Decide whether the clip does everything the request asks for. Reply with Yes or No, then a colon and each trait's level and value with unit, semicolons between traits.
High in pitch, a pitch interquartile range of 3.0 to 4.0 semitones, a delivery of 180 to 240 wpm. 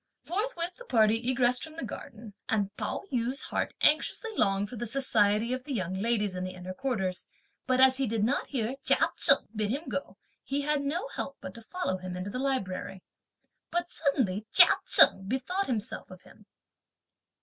No: high, 240 Hz; average, 5.3 semitones; average, 185 wpm